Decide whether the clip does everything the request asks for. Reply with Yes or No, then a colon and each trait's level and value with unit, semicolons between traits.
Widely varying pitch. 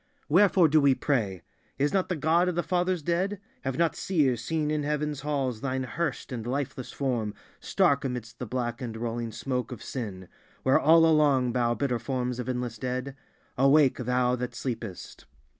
No: average, 3.7 semitones